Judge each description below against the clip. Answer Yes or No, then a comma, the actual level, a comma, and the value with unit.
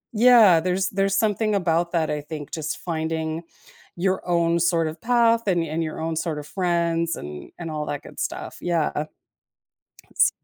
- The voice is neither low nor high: Yes, medium, 170 Hz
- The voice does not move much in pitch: No, average, 3.0 semitones